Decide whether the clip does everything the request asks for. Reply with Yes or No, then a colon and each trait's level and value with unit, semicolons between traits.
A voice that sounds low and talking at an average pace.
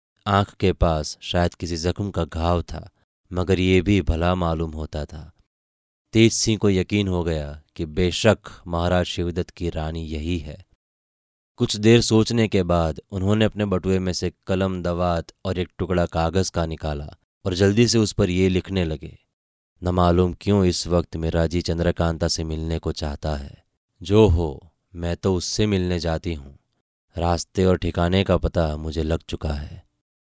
Yes: very low, 85 Hz; average, 170 wpm